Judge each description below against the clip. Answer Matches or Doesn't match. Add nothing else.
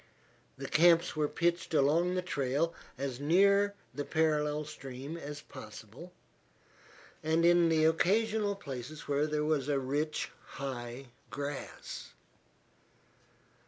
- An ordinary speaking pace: Doesn't match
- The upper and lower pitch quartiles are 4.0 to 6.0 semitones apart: Doesn't match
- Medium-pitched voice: Matches